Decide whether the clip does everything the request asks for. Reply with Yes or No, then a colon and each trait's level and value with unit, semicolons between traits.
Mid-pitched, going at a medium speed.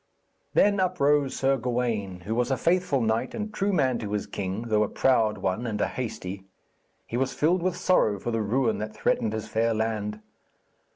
No: low, 115 Hz; average, 190 wpm